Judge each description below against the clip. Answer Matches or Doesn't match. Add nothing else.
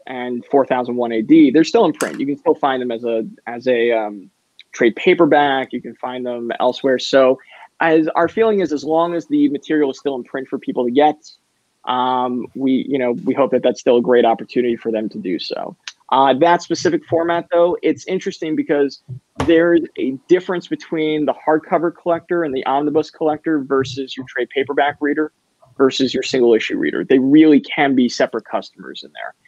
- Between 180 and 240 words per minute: Matches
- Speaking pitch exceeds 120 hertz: Matches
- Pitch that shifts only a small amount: Doesn't match